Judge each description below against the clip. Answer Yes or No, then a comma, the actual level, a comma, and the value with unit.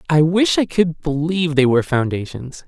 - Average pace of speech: Yes, average, 180 wpm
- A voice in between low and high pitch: Yes, medium, 160 Hz